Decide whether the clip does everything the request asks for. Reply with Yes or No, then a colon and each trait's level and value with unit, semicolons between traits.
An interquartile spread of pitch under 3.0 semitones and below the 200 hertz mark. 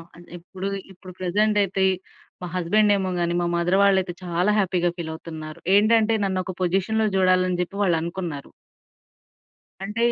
Yes: narrow, 2.4 semitones; medium, 185 Hz